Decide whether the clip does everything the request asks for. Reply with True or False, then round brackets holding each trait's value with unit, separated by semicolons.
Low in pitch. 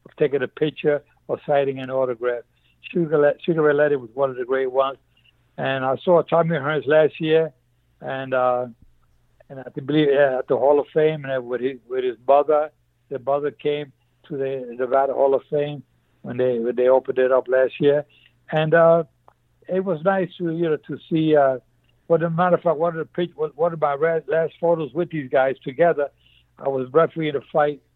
False (145 Hz)